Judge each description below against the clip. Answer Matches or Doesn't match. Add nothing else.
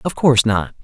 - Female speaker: Doesn't match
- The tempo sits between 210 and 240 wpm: Matches